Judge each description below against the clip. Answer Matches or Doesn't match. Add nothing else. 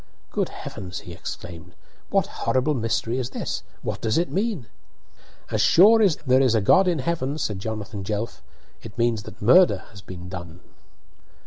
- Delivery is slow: Doesn't match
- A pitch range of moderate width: Doesn't match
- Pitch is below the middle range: Matches